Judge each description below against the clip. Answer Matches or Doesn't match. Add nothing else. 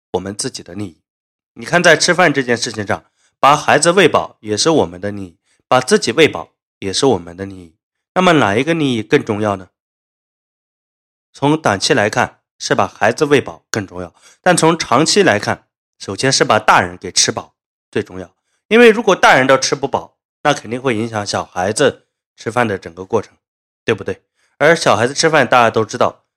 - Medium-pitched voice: Doesn't match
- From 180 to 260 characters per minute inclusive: Doesn't match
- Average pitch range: Doesn't match